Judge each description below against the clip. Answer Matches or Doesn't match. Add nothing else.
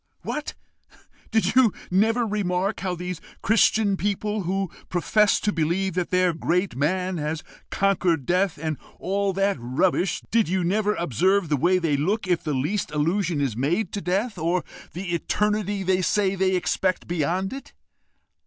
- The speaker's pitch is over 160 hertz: Matches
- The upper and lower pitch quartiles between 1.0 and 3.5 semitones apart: Matches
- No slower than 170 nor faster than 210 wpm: Doesn't match